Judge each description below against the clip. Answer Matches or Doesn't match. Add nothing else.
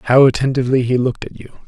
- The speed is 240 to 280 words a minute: Doesn't match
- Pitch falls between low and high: Doesn't match